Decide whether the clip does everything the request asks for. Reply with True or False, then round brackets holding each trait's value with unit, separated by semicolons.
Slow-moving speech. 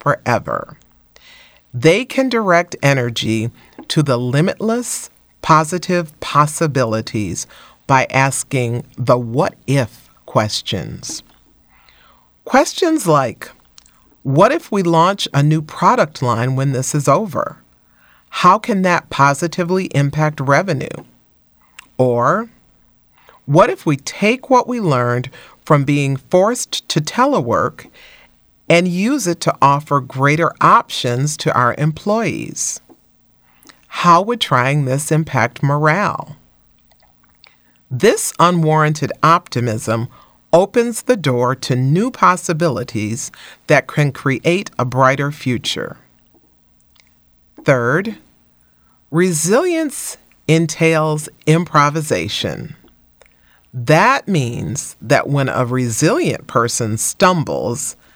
True (95 wpm)